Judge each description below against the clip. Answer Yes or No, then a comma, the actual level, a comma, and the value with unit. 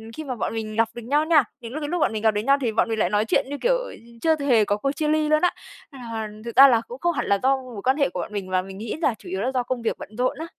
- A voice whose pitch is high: Yes, very high, 250 Hz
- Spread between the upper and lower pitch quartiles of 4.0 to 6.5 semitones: Yes, average, 4.9 semitones